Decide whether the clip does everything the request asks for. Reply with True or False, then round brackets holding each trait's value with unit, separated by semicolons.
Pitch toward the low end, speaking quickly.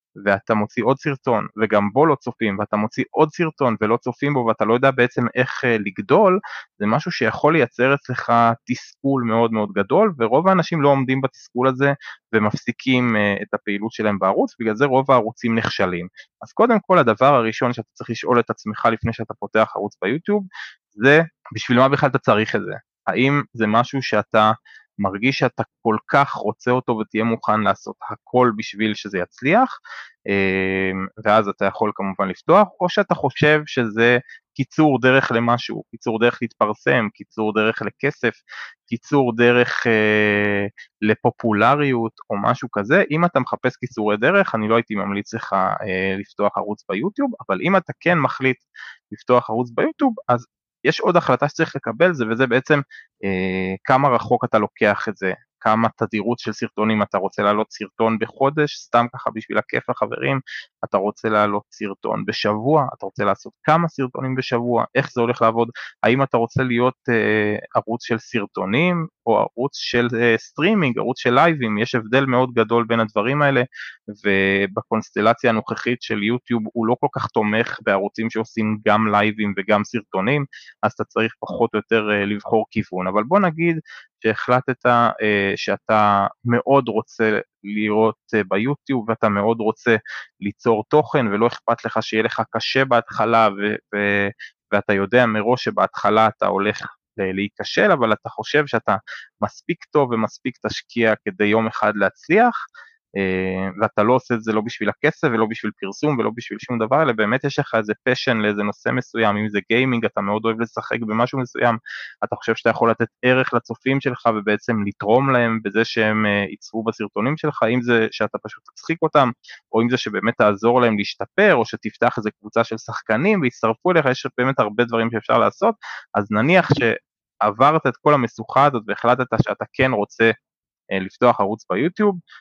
True (115 Hz; 165 wpm)